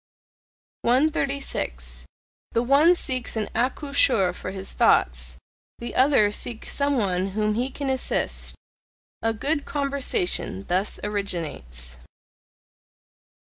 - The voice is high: Yes, high, 220 Hz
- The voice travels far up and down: Yes, wide, 7.1 semitones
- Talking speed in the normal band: No, slow, 100 wpm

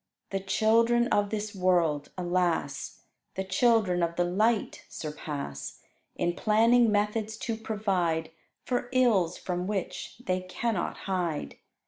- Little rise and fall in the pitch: No, average, 4.0 semitones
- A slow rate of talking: Yes, slow, 120 wpm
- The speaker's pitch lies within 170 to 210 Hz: Yes, high, 190 Hz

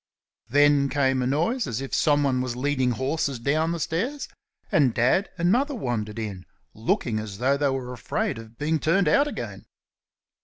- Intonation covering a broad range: No, average, 4.7 semitones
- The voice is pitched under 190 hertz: Yes, medium, 140 Hz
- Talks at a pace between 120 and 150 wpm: No, average, 170 wpm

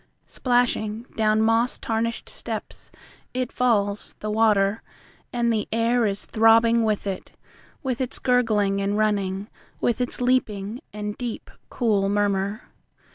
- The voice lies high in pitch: Yes, high, 220 Hz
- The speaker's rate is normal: No, slow, 130 wpm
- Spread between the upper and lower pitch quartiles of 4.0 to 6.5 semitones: No, narrow, 2.5 semitones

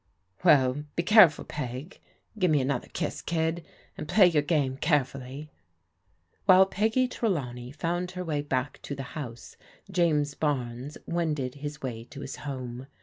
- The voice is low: No, medium, 145 Hz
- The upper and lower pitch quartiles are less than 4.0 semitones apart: No, average, 4.6 semitones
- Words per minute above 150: No, average, 145 wpm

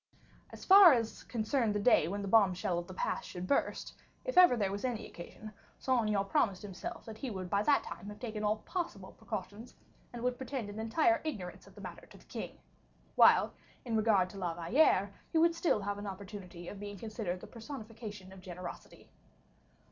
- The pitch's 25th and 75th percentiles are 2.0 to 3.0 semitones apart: No, average, 3.9 semitones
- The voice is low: No, high, 210 Hz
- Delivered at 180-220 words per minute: Yes, average, 200 wpm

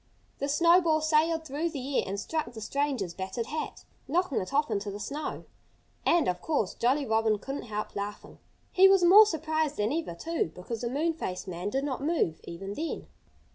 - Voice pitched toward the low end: No, very high, 280 Hz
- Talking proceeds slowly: No, average, 190 wpm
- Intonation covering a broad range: Yes, wide, 7.4 semitones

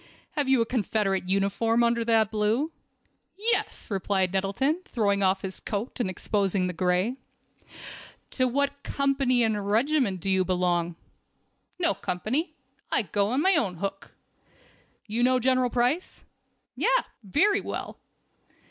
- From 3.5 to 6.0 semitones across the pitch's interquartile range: Yes, wide, 5.4 semitones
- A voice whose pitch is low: No, high, 225 Hz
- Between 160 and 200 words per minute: No, average, 140 wpm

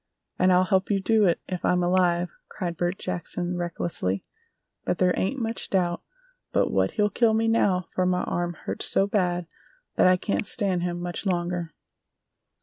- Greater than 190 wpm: No, average, 175 wpm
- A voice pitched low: No, medium, 180 Hz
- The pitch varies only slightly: Yes, narrow, 2.1 semitones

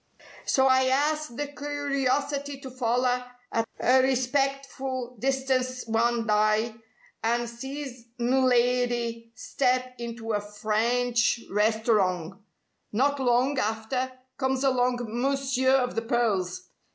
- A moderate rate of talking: No, slow, 110 wpm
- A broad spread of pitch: No, narrow, 2.5 semitones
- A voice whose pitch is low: No, very high, 250 Hz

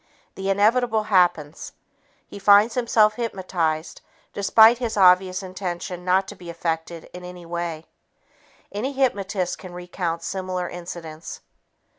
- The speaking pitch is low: No, medium, 185 Hz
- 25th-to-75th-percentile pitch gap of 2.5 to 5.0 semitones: Yes, average, 3.2 semitones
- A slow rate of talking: Yes, slow, 120 wpm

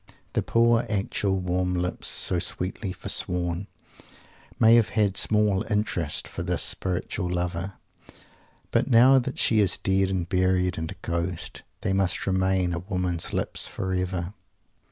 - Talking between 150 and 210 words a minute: No, average, 140 wpm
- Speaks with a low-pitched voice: Yes, very low, 95 Hz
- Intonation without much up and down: Yes, narrow, 2.2 semitones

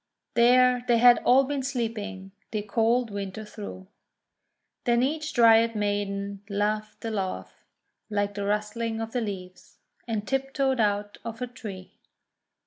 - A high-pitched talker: Yes, high, 220 Hz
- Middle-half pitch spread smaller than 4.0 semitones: Yes, average, 3.0 semitones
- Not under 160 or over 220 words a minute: No, slow, 135 wpm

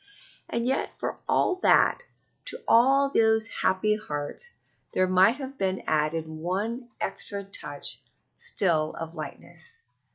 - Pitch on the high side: Yes, high, 200 Hz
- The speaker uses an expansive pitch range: Yes, wide, 7.4 semitones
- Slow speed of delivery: Yes, slow, 125 wpm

